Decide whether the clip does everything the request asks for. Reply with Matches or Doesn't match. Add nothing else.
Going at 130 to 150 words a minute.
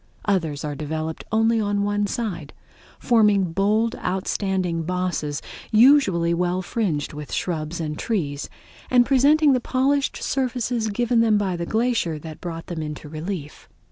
Matches